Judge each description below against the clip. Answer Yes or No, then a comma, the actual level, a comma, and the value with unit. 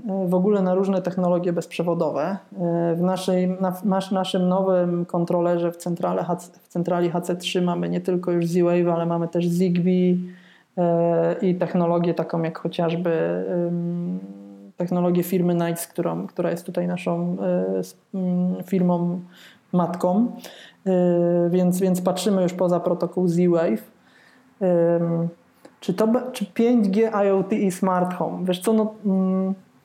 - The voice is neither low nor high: Yes, medium, 180 Hz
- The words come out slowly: No, average, 135 wpm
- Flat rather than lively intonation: Yes, narrow, 1.5 semitones